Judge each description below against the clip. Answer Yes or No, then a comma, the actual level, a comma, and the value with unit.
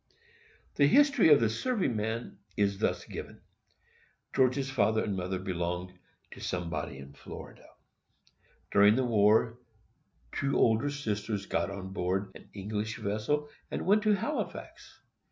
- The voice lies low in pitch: Yes, low, 110 Hz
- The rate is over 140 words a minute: No, slow, 135 wpm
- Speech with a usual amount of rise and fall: No, wide, 5.9 semitones